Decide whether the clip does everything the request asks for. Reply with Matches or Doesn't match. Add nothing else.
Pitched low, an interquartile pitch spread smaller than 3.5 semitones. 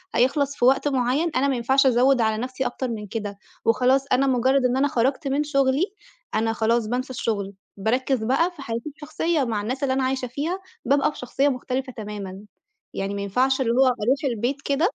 Doesn't match